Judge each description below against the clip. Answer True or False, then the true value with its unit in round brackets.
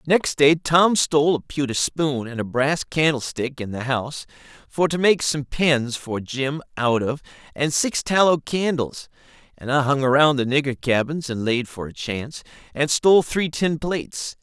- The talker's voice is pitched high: False (140 Hz)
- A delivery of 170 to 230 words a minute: True (185 wpm)